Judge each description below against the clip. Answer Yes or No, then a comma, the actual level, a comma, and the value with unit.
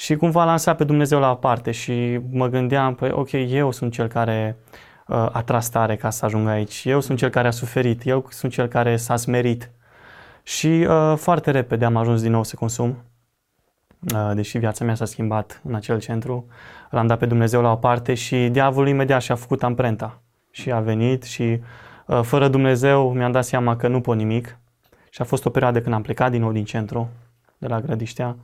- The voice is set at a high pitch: No, low, 120 Hz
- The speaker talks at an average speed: No, fast, 210 wpm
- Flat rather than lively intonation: Yes, narrow, 2.1 semitones